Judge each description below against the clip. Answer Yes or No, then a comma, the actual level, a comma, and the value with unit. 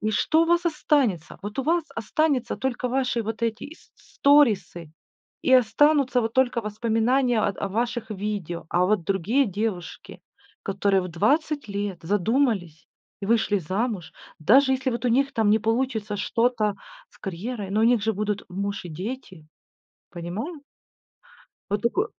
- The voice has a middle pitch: No, high, 220 Hz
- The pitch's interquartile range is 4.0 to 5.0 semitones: Yes, average, 4.6 semitones